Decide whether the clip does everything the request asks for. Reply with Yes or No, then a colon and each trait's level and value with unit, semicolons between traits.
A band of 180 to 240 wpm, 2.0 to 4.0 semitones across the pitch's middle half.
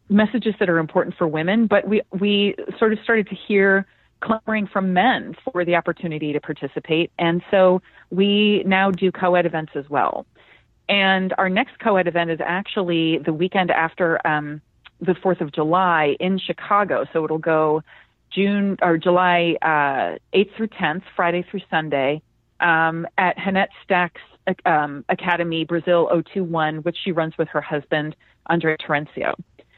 No: average, 155 wpm; average, 3.3 semitones